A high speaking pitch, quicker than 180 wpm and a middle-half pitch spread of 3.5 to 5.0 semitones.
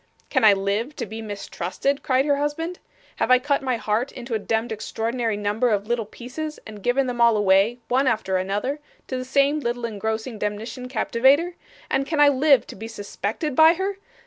Yes: high, 240 Hz; average, 195 wpm; average, 4.3 semitones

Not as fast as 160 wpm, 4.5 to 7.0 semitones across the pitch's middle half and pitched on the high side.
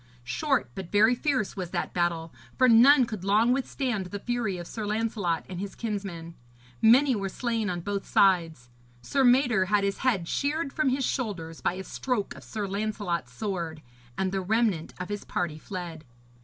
No: average, 180 wpm; average, 5.1 semitones; high, 205 Hz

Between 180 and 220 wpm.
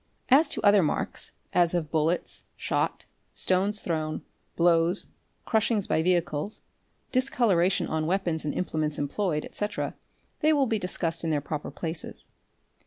No: slow, 135 wpm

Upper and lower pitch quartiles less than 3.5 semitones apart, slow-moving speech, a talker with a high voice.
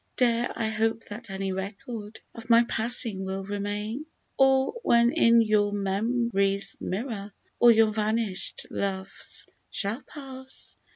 Yes: average, 2.9 semitones; slow, 125 wpm; high, 220 Hz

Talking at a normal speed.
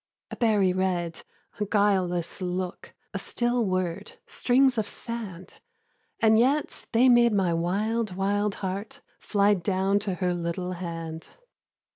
No: slow, 130 wpm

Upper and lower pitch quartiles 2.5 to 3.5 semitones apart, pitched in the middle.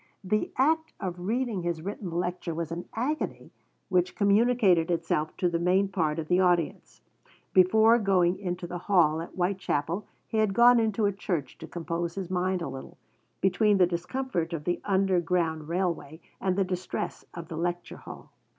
Yes: average, 2.8 semitones; medium, 180 Hz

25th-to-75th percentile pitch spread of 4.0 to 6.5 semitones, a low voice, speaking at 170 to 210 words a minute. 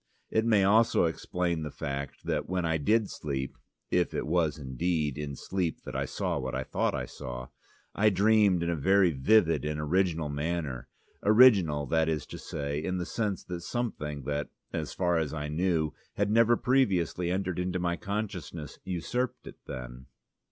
Yes: average, 4.7 semitones; very low, 85 Hz; average, 175 wpm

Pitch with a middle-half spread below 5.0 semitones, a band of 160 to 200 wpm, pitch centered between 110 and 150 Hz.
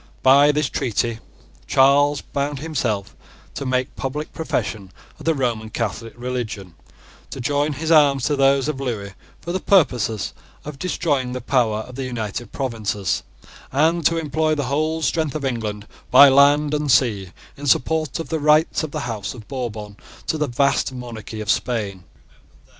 Yes: average, 4.5 semitones; average, 165 wpm; low, 135 Hz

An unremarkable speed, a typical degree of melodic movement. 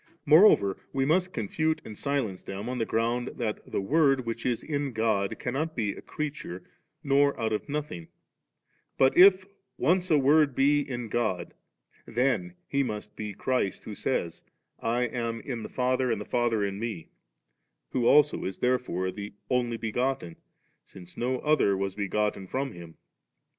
Yes: average, 170 wpm; average, 4.9 semitones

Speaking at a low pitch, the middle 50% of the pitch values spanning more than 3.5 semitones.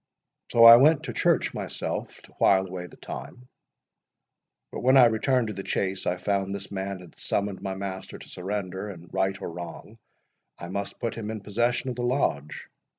Yes: low, 100 Hz; average, 3.9 semitones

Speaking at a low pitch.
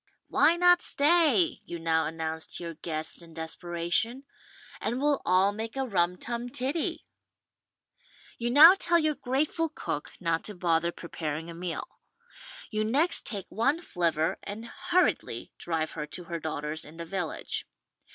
No: medium, 185 Hz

